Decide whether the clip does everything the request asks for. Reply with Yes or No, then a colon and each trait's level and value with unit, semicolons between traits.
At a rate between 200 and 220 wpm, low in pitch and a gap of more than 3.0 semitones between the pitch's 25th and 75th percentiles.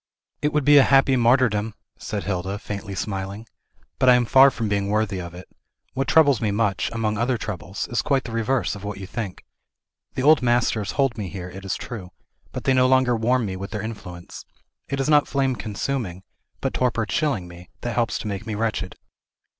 Yes: fast, 205 wpm; low, 110 Hz; average, 4.6 semitones